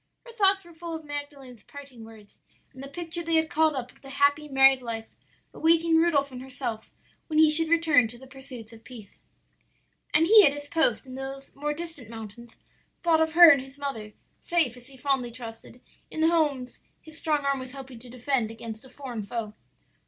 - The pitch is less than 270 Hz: No, very high, 275 Hz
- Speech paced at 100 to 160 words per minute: No, fast, 205 wpm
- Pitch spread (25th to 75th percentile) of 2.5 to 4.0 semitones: No, average, 4.4 semitones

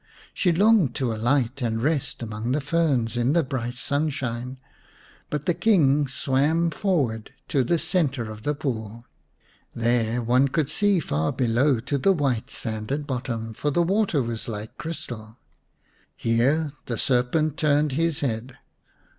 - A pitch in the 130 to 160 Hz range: Yes, low, 135 Hz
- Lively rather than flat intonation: No, average, 4.6 semitones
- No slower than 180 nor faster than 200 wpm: No, average, 145 wpm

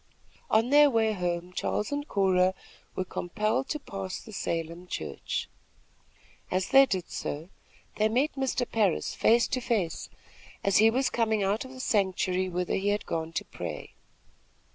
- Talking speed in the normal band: Yes, average, 160 wpm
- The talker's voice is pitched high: Yes, high, 205 Hz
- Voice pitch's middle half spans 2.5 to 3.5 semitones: No, average, 4.7 semitones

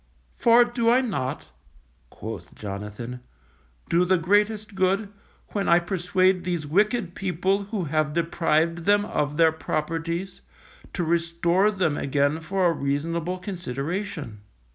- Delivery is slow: Yes, slow, 125 wpm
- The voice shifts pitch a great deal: No, average, 4.0 semitones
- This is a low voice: No, medium, 170 Hz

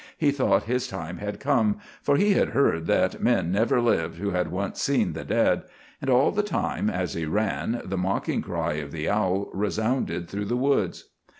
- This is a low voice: Yes, low, 105 Hz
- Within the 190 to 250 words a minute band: Yes, average, 195 wpm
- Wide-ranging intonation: Yes, wide, 5.7 semitones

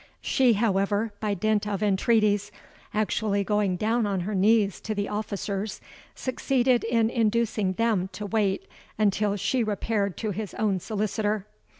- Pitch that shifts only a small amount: Yes, narrow, 1.8 semitones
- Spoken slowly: Yes, slow, 130 wpm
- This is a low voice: No, high, 210 Hz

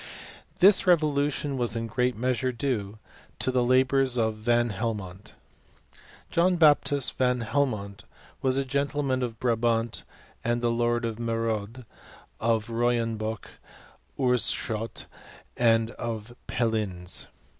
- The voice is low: Yes, low, 120 Hz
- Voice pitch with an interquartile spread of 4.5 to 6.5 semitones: No, narrow, 2.5 semitones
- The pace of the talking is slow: Yes, slow, 115 wpm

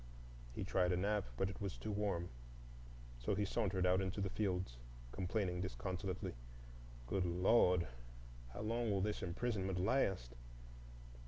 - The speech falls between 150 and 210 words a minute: No, average, 140 wpm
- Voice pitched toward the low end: Yes, very low, 95 Hz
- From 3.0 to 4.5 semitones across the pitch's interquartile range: No, narrow, 2.4 semitones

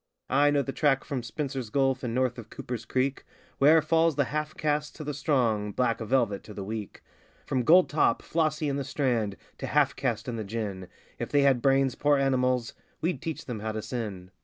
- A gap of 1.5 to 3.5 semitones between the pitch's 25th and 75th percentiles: No, average, 4.1 semitones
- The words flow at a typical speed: No, fast, 210 wpm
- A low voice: Yes, low, 130 Hz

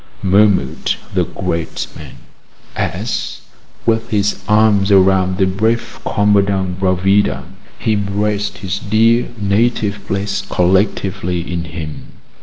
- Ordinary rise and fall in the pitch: No, narrow, 2.1 semitones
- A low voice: Yes, low, 100 Hz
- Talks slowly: Yes, slow, 105 wpm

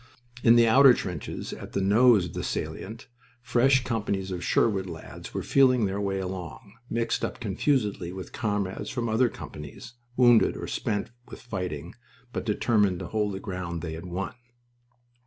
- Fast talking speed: No, average, 165 wpm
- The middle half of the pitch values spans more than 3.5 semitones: Yes, average, 4.1 semitones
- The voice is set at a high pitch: No, low, 100 Hz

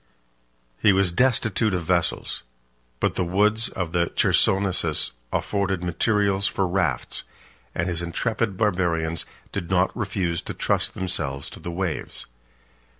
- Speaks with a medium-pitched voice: No, very low, 95 Hz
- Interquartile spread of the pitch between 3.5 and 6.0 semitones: No, average, 2.8 semitones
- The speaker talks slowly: Yes, slow, 130 wpm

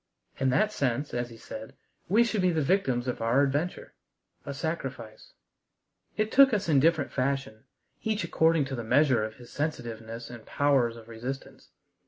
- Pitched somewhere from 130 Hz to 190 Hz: Yes, low, 135 Hz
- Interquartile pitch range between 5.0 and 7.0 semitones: Yes, wide, 5.5 semitones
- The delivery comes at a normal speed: Yes, average, 170 wpm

